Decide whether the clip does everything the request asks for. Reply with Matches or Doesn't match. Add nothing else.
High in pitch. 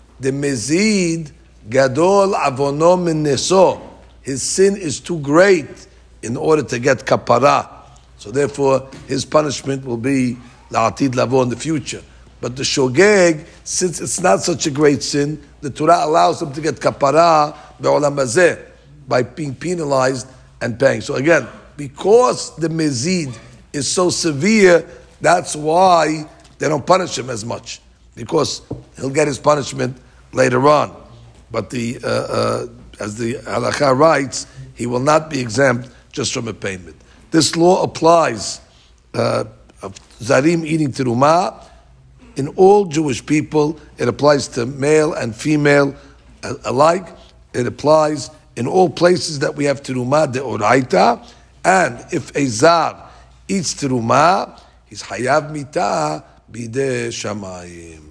Doesn't match